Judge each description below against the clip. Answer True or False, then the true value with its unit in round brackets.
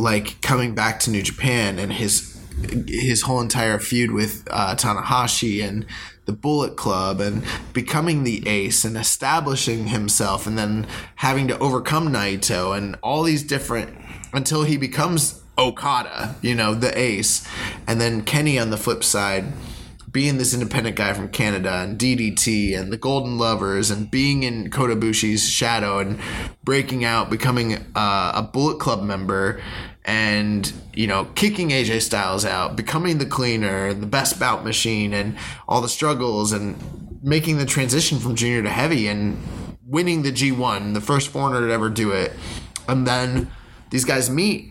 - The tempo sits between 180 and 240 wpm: False (160 wpm)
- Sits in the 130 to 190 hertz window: False (115 Hz)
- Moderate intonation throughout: True (3.9 semitones)